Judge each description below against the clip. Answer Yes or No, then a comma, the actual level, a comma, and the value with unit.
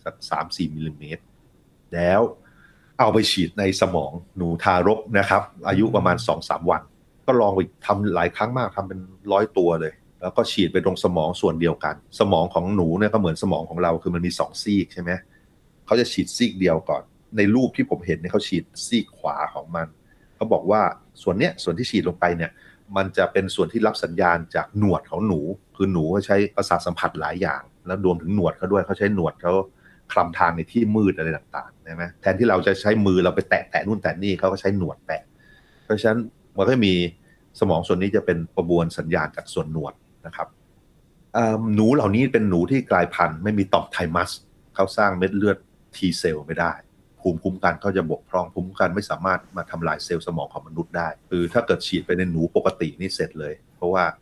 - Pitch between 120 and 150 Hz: No, very low, 95 Hz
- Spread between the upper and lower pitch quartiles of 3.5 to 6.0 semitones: No, average, 2.8 semitones